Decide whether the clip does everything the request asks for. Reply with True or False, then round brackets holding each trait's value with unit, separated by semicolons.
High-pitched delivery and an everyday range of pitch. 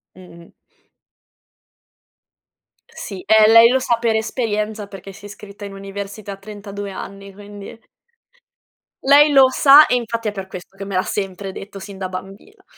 False (205 Hz; 2.2 semitones)